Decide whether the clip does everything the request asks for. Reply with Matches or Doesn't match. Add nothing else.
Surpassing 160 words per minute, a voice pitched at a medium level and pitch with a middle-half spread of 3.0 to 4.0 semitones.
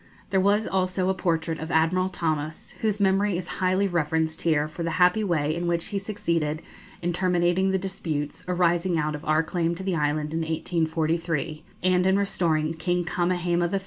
Doesn't match